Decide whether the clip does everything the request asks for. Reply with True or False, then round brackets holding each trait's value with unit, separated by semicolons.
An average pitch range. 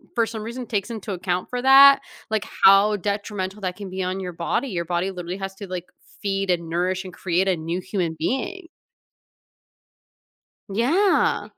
True (3.3 semitones)